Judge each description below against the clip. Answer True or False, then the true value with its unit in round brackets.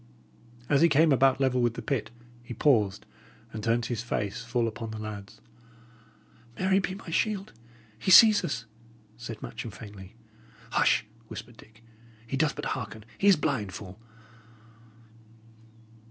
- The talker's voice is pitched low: True (120 Hz)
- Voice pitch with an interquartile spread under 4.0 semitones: False (5.2 semitones)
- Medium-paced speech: True (145 wpm)